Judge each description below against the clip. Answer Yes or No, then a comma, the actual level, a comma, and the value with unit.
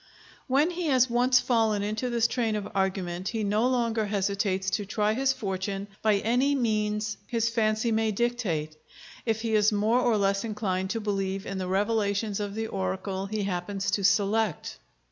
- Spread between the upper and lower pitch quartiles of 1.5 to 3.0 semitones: Yes, average, 2.7 semitones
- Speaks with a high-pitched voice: Yes, high, 210 Hz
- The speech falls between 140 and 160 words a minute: No, average, 175 wpm